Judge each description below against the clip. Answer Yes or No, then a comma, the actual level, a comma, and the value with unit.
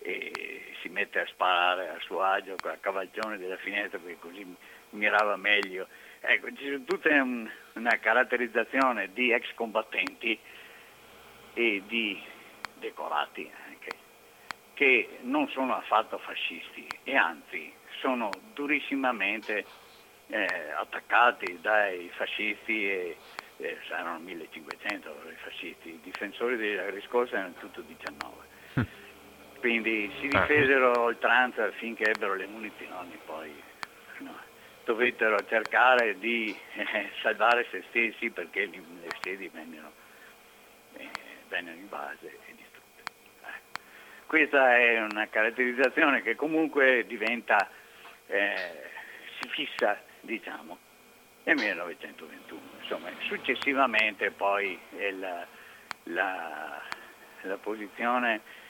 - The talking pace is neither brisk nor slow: No, slow, 105 wpm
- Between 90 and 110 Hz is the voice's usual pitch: No, low, 120 Hz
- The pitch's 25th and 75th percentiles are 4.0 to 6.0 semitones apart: Yes, average, 5.2 semitones